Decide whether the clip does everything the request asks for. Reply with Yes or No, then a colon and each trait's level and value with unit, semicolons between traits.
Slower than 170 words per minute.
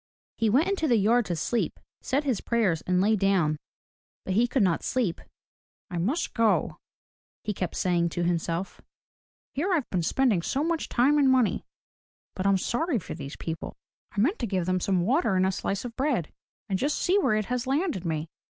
No: average, 200 wpm